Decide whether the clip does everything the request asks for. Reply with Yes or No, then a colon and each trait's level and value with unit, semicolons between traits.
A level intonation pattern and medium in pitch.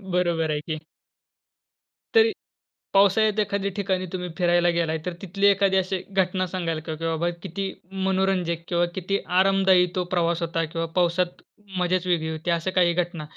Yes: narrow, 2.2 semitones; medium, 180 Hz